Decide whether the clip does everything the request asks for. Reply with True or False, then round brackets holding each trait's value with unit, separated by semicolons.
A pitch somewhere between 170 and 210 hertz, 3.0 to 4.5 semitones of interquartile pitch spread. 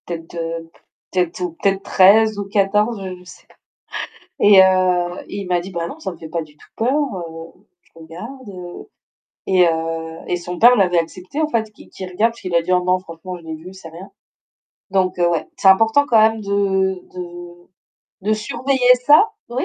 True (185 Hz; 3.3 semitones)